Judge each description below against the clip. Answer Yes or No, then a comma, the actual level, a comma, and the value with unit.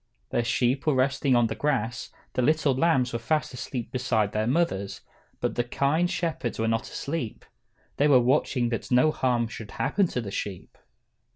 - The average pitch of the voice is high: No, low, 125 Hz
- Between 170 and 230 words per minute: Yes, average, 180 wpm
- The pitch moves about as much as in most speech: Yes, average, 4.0 semitones